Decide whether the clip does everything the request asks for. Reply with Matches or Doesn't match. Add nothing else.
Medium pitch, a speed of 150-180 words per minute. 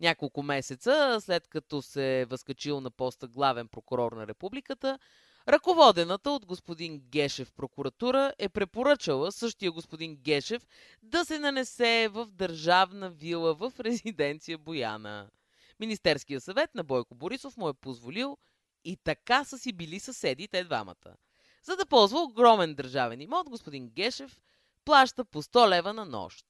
Doesn't match